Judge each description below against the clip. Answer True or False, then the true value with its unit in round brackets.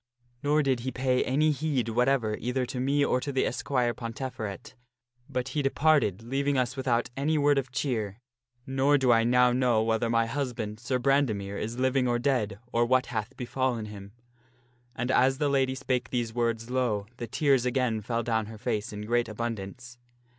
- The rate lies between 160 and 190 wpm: True (185 wpm)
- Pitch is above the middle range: False (125 Hz)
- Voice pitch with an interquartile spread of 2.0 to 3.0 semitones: True (2.7 semitones)